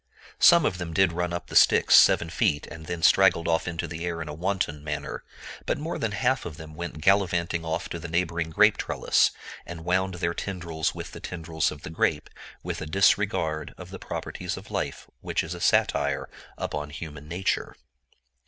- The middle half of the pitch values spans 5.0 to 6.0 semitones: No, narrow, 2.4 semitones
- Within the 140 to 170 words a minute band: No, average, 195 wpm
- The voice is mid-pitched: No, very low, 85 Hz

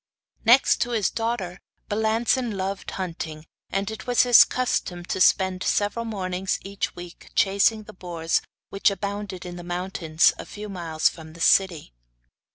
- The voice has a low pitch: No, high, 195 Hz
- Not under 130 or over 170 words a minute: Yes, average, 155 wpm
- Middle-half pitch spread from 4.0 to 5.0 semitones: No, average, 3.4 semitones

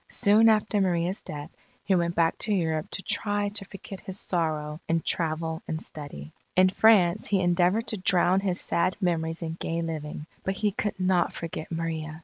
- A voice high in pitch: No, medium, 175 Hz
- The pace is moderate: Yes, average, 180 wpm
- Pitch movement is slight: No, average, 3.2 semitones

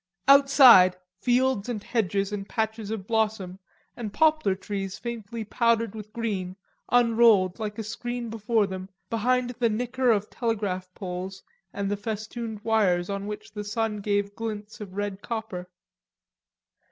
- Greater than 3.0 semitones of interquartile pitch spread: No, average, 2.7 semitones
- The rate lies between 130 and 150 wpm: Yes, average, 140 wpm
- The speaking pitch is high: Yes, high, 215 Hz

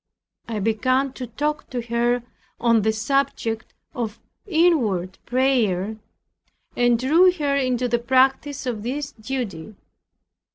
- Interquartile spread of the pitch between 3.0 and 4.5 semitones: Yes, average, 3.6 semitones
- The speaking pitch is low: No, high, 245 Hz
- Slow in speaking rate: Yes, slow, 120 wpm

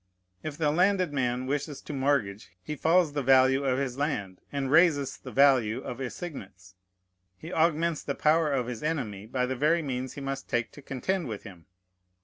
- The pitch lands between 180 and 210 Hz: No, low, 135 Hz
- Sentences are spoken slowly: No, average, 185 wpm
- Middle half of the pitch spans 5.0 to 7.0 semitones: No, average, 3.5 semitones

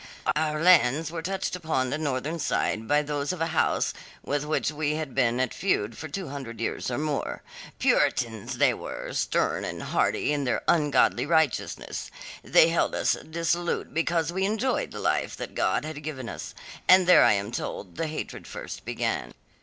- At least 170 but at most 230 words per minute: Yes, average, 180 wpm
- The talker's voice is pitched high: No, medium, 150 Hz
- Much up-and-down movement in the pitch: No, average, 4.0 semitones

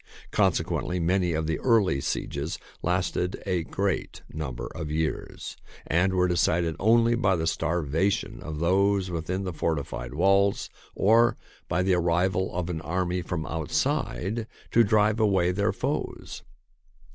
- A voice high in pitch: No, very low, 90 Hz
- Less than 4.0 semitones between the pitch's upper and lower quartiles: Yes, average, 3.2 semitones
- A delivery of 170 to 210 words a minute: No, average, 140 wpm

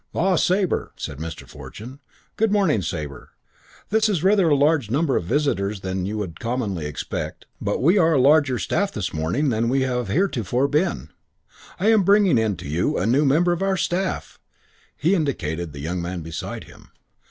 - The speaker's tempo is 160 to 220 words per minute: Yes, average, 185 wpm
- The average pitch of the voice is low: Yes, low, 130 Hz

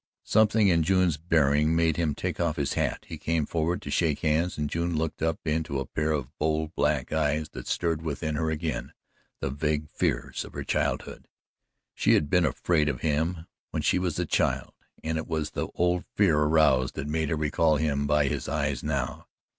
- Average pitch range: No, narrow, 1.8 semitones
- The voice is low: Yes, very low, 80 Hz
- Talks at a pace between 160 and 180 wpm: No, average, 200 wpm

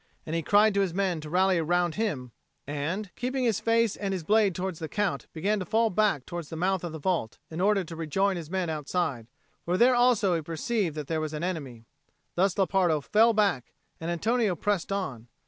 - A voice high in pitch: No, medium, 180 Hz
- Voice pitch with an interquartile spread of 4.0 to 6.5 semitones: Yes, average, 4.4 semitones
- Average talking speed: No, fast, 215 wpm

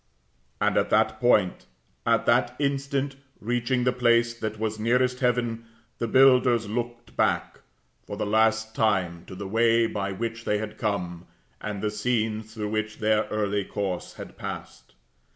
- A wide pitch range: No, narrow, 2.4 semitones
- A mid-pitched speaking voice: No, low, 110 Hz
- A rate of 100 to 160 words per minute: Yes, average, 155 wpm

